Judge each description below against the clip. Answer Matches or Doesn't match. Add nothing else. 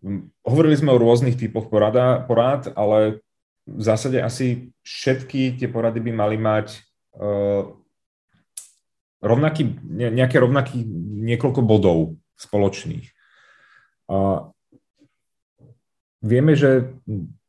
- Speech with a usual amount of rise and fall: Matches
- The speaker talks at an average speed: Doesn't match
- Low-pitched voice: Matches